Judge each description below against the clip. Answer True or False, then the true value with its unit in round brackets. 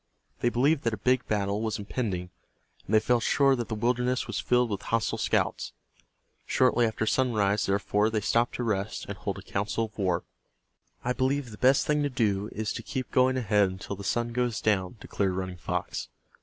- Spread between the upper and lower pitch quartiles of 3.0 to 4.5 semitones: True (3.5 semitones)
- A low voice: True (110 Hz)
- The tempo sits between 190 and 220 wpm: True (195 wpm)